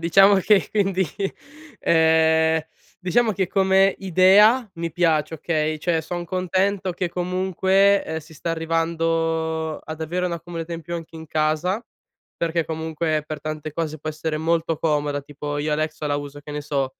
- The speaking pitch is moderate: Yes, medium, 165 Hz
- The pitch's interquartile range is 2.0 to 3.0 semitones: Yes, average, 2.7 semitones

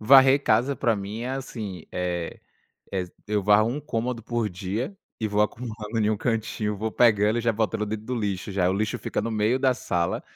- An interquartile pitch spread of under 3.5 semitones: Yes, narrow, 2.5 semitones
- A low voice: Yes, low, 110 Hz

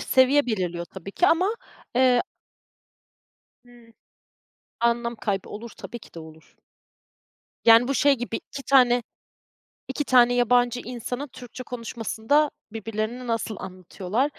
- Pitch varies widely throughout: No, narrow, 2.5 semitones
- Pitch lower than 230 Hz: No, high, 240 Hz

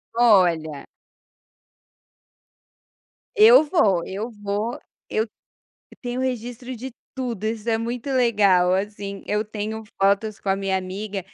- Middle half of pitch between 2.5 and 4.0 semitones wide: Yes, average, 3.6 semitones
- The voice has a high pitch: Yes, high, 215 Hz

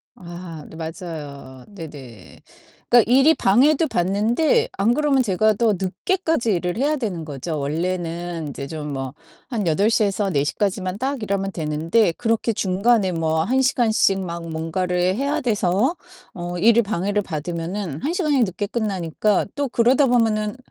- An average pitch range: No, wide, 5.8 semitones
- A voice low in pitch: No, high, 195 Hz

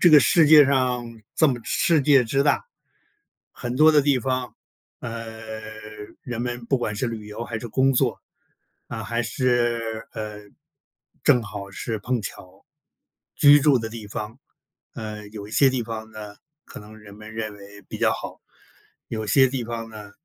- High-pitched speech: No, low, 115 Hz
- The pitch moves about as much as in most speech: Yes, average, 3.2 semitones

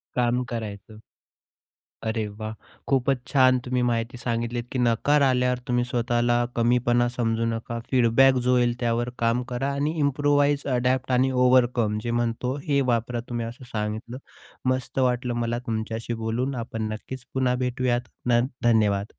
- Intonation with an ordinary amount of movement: No, narrow, 1.6 semitones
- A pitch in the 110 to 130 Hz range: Yes, low, 120 Hz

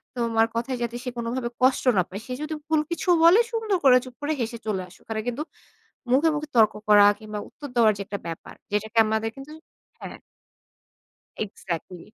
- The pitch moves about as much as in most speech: Yes, average, 4.3 semitones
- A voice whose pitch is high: Yes, high, 235 Hz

